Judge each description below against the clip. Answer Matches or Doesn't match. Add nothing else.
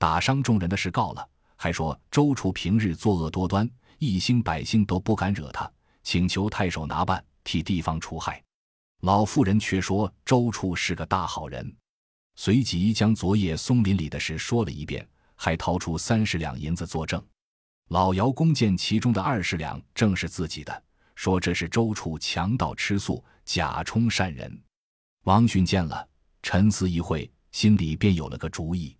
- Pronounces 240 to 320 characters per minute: Matches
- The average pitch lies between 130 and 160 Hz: Doesn't match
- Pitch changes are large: Doesn't match